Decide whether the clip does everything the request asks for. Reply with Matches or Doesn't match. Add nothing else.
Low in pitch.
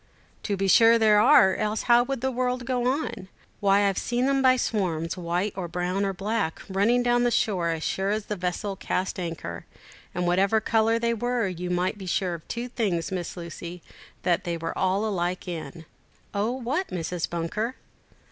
Doesn't match